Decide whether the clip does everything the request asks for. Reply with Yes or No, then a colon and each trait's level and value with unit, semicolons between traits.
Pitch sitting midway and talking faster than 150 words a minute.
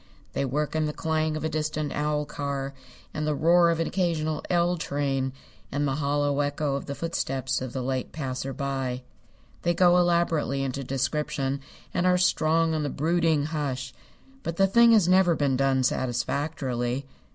Yes: medium, 150 Hz; average, 175 wpm